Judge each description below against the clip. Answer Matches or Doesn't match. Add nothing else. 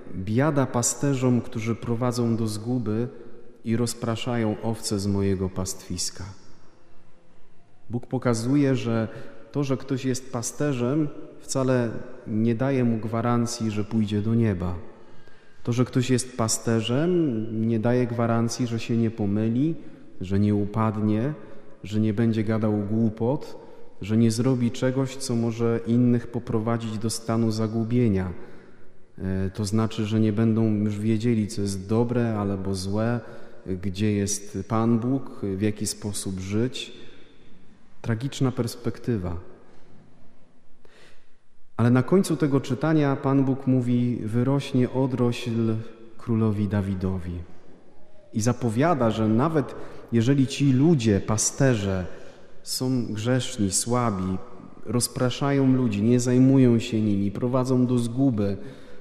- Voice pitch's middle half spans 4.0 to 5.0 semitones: Doesn't match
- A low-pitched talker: Matches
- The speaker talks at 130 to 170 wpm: Doesn't match